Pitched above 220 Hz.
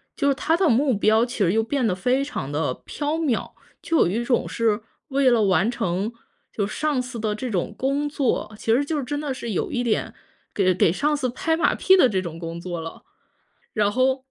Yes: high, 240 Hz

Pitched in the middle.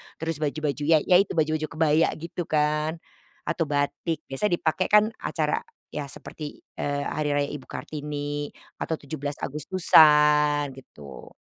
Yes: medium, 150 Hz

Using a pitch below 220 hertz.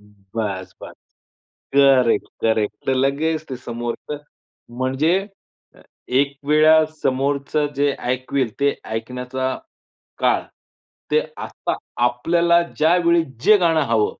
Yes: low, 135 Hz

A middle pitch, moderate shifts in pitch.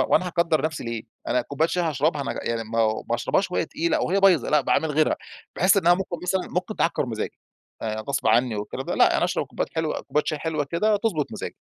No: medium, 155 Hz; wide, 6.3 semitones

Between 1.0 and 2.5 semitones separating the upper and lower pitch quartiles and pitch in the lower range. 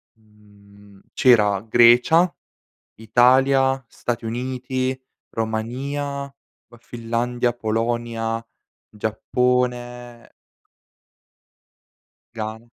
Yes: narrow, 2.2 semitones; low, 120 Hz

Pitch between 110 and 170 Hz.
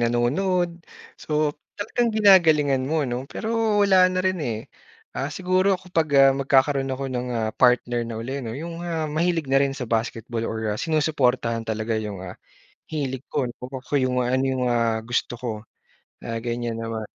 Yes: low, 135 Hz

